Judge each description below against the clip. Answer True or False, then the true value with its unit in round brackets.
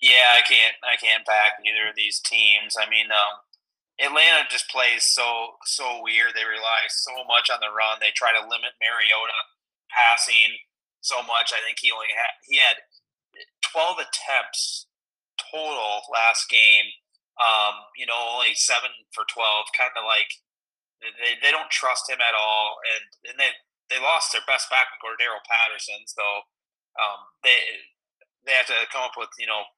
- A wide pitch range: False (3.0 semitones)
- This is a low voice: True (115 Hz)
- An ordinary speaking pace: True (170 wpm)